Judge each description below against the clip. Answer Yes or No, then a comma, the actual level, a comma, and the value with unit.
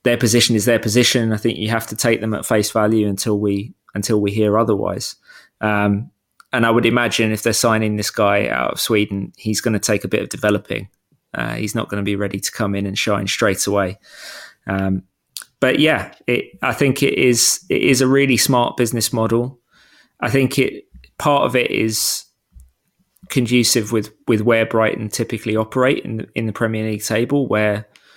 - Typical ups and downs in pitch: No, narrow, 2.3 semitones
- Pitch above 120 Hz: No, low, 110 Hz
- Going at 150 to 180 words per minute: No, average, 200 wpm